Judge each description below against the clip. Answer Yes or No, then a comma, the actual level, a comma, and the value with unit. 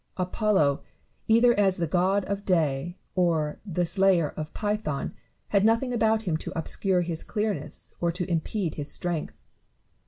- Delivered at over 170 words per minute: No, average, 150 wpm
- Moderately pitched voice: Yes, medium, 180 Hz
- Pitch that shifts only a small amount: No, average, 4.1 semitones